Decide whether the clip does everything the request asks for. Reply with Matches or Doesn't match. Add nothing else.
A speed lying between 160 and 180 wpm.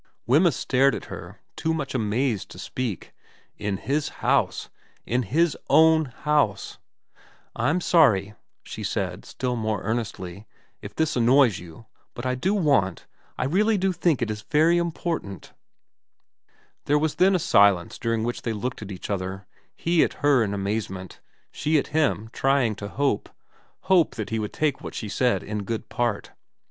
Matches